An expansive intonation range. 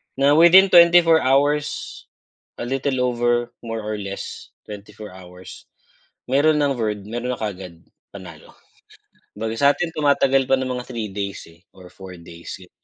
Yes: wide, 6.2 semitones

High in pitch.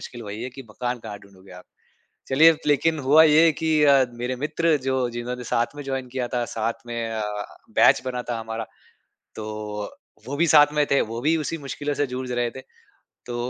No: low, 125 Hz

